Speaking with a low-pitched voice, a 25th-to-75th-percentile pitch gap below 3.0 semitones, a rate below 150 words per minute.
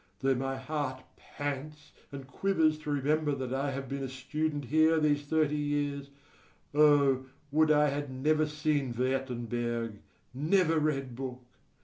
No: medium, 145 Hz; narrow, 2.5 semitones; average, 140 wpm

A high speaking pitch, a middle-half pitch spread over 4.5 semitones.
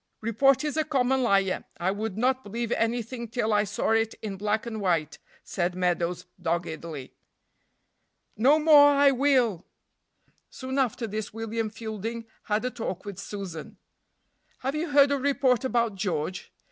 Yes: high, 225 Hz; average, 4.9 semitones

